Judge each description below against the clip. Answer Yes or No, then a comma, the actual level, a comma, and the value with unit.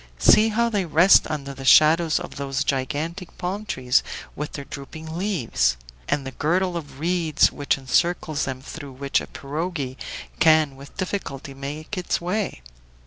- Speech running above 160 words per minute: No, average, 155 wpm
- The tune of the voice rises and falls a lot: No, average, 4.3 semitones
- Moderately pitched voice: Yes, medium, 155 Hz